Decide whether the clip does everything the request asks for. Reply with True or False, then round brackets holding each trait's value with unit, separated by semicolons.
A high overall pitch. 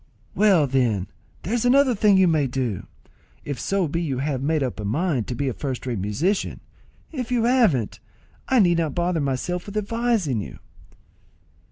False (160 Hz)